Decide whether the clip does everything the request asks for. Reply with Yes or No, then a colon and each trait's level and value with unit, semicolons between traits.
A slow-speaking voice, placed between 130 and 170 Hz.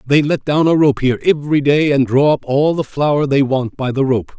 No: fast, 260 wpm; medium, 140 Hz